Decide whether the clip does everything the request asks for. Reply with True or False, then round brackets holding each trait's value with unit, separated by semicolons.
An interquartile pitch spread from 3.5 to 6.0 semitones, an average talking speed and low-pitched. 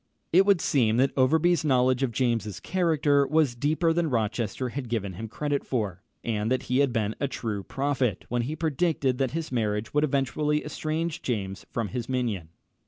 True (4.8 semitones; 180 wpm; 130 Hz)